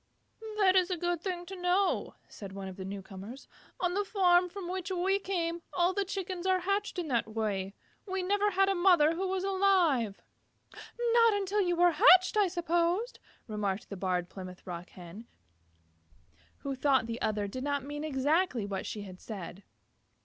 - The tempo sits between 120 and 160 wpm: No, average, 185 wpm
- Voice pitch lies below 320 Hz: No, very high, 345 Hz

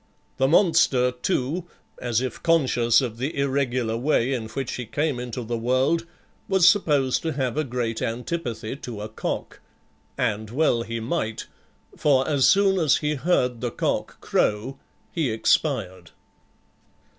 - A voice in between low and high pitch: No, low, 130 Hz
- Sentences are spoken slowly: No, average, 145 wpm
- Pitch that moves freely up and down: No, average, 4.2 semitones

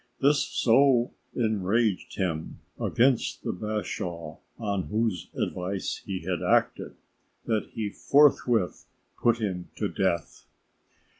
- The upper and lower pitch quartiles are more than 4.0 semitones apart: Yes, average, 4.5 semitones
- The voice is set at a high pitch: No, low, 105 Hz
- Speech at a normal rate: No, slow, 105 wpm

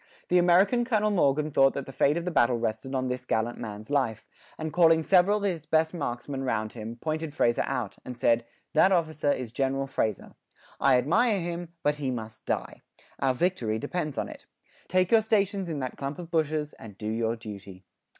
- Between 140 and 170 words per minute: No, average, 200 wpm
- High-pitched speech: No, medium, 145 Hz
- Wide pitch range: Yes, wide, 6.5 semitones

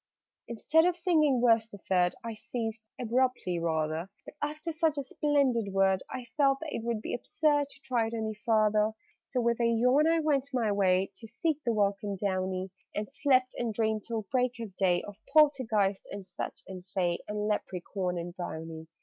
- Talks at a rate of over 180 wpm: Yes, average, 190 wpm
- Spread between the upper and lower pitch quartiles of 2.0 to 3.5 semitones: No, wide, 5.4 semitones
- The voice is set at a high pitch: Yes, high, 225 Hz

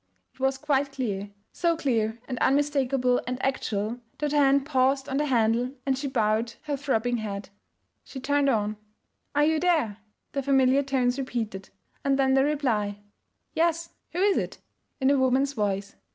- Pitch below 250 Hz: No, very high, 265 Hz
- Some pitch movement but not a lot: Yes, average, 3.5 semitones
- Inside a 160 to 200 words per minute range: Yes, average, 165 wpm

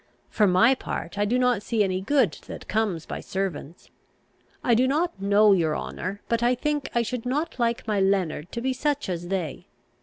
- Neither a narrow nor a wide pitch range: Yes, average, 5.0 semitones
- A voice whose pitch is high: Yes, high, 215 Hz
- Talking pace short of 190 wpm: No, average, 195 wpm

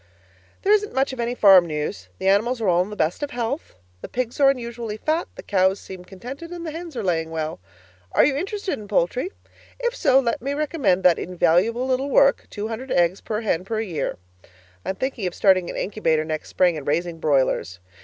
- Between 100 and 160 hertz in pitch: No, high, 215 Hz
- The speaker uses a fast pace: Yes, fast, 210 wpm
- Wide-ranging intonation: Yes, wide, 7.1 semitones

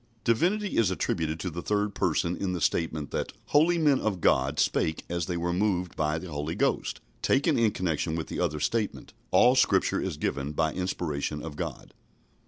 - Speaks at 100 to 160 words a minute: No, average, 190 wpm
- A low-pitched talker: Yes, very low, 90 Hz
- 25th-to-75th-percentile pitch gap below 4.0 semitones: No, average, 5.3 semitones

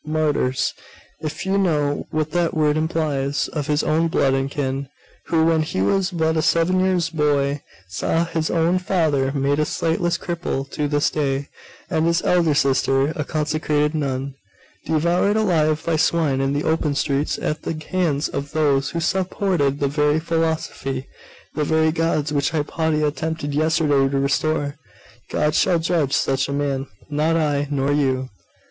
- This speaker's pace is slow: No, average, 165 wpm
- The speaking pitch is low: No, medium, 150 Hz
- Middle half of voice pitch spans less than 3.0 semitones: Yes, narrow, 2.5 semitones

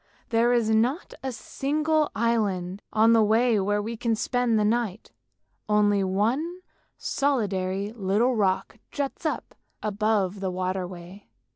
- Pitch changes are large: No, average, 3.6 semitones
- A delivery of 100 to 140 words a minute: Yes, slow, 135 wpm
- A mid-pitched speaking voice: No, high, 220 Hz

